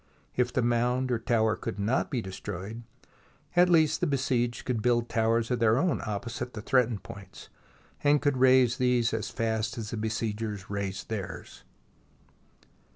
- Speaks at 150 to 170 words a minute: Yes, average, 160 wpm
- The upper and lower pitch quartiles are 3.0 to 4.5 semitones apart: No, narrow, 2.5 semitones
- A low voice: Yes, low, 115 Hz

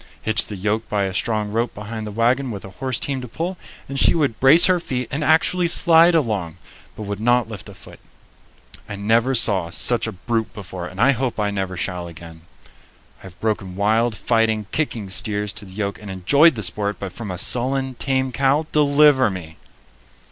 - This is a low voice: Yes, low, 110 Hz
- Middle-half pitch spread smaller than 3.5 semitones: No, average, 4.8 semitones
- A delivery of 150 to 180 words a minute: No, average, 200 wpm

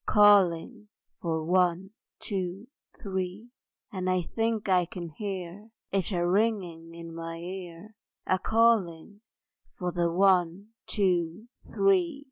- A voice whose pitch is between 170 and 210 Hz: Yes, medium, 185 Hz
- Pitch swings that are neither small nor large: Yes, average, 3.3 semitones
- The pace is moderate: No, slow, 115 wpm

